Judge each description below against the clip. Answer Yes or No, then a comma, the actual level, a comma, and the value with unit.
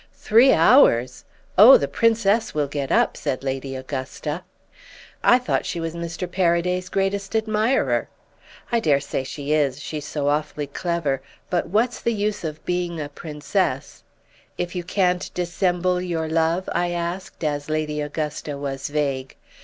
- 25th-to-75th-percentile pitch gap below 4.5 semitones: Yes, average, 4.0 semitones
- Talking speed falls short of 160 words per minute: Yes, average, 145 wpm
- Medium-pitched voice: Yes, medium, 165 Hz